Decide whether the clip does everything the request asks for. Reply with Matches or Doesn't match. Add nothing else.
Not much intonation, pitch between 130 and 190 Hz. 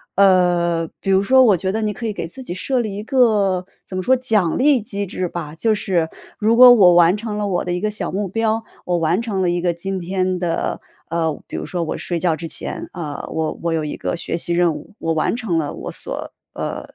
Doesn't match